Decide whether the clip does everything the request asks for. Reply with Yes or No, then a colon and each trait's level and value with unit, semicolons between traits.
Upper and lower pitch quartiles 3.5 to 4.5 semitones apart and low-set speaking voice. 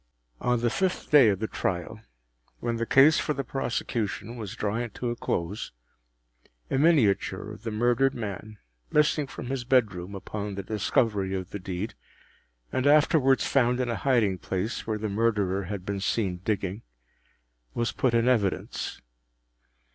Yes: average, 4.1 semitones; low, 110 Hz